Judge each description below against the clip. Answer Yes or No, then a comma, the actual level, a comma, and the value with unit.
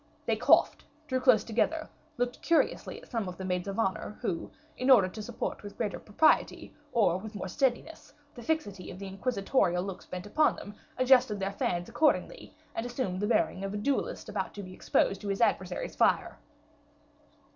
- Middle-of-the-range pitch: No, high, 210 Hz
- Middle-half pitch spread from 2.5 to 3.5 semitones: No, average, 4.7 semitones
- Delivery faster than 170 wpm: Yes, average, 185 wpm